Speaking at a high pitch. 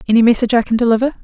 Yes: high, 235 Hz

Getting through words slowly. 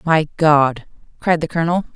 No: average, 155 wpm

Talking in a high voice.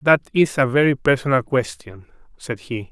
No: low, 130 Hz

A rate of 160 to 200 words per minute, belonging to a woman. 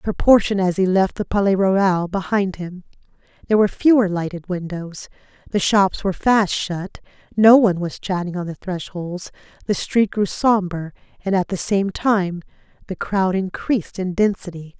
Yes: average, 165 wpm; female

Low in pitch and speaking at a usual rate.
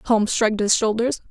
No: high, 220 Hz; average, 185 wpm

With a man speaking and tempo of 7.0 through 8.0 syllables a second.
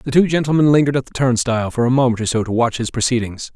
Yes: male; 7.1 syllables/s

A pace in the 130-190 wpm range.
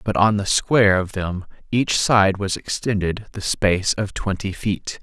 Yes: average, 180 wpm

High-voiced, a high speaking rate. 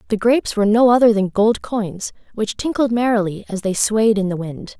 Yes: high, 215 Hz; fast, 215 wpm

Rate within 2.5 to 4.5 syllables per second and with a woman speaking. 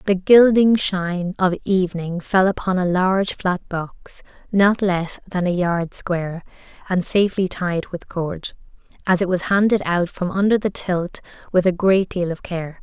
Yes: 4.4 syllables/s; female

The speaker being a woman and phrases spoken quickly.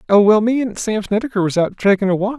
No: male; fast, 275 wpm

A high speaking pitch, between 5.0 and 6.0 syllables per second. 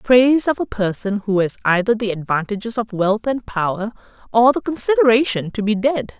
Yes: high, 225 Hz; 5.4 syllables/s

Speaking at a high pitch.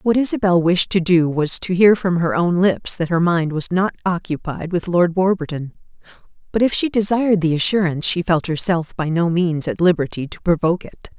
No: medium, 175 Hz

